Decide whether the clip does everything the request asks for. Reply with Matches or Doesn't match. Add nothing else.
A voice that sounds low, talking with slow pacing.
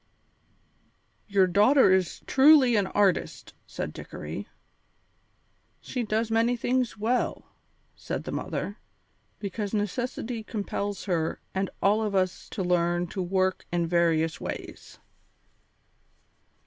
Doesn't match